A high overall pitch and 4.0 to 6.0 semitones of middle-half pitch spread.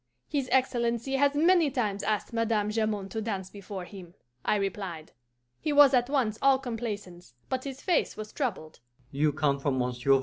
Yes: high, 225 Hz; average, 4.9 semitones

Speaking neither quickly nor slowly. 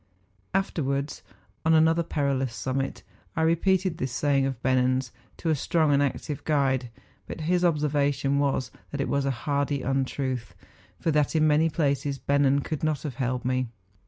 Yes: average, 160 wpm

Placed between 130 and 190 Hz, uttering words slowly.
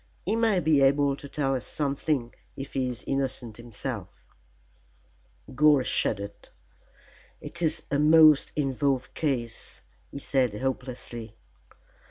Yes: low, 135 Hz; slow, 120 wpm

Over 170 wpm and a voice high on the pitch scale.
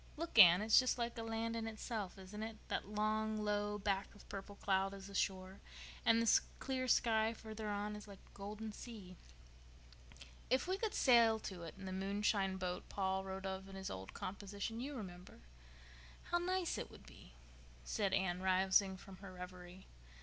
Yes: average, 180 wpm; high, 200 Hz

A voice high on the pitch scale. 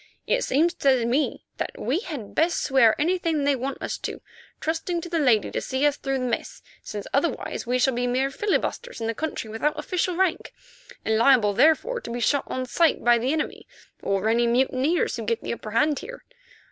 Yes: very high, 270 Hz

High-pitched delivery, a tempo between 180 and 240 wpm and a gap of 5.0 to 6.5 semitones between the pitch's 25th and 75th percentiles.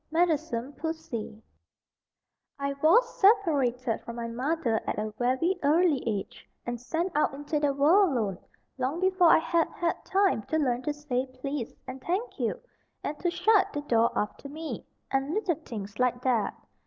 No: very high, 290 Hz; average, 165 wpm; average, 5.3 semitones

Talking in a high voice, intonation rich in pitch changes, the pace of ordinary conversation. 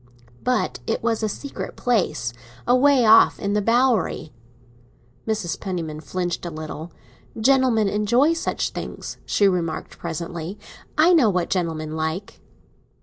No: high, 200 Hz; wide, 6.5 semitones; slow, 125 wpm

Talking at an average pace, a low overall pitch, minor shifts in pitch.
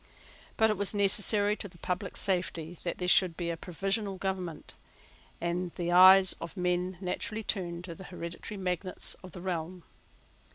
No: average, 165 wpm; medium, 180 Hz; narrow, 2.0 semitones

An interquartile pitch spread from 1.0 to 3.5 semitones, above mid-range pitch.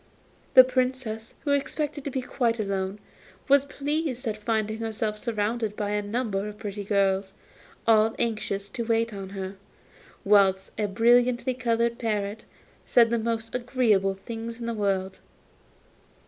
Yes: average, 2.9 semitones; high, 225 Hz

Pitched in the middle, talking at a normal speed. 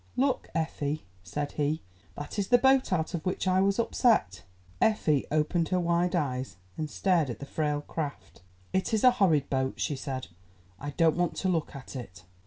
Yes: medium, 160 Hz; average, 190 wpm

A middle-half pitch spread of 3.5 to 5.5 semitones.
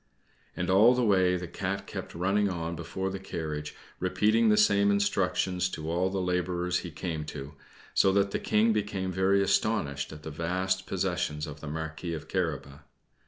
No: average, 3.1 semitones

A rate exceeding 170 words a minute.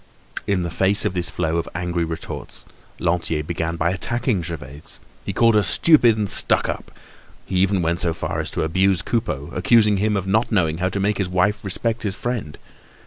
Yes: average, 195 wpm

